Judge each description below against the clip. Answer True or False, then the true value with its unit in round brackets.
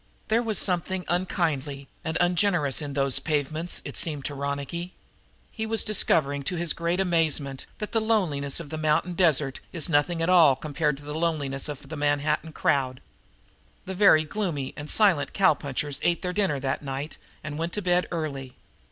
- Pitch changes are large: False (3.9 semitones)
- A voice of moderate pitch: True (155 Hz)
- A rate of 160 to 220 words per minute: True (180 wpm)